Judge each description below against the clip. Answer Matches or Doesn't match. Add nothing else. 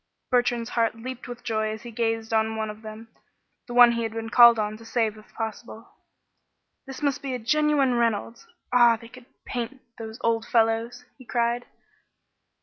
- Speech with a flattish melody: Matches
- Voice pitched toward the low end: Doesn't match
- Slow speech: Doesn't match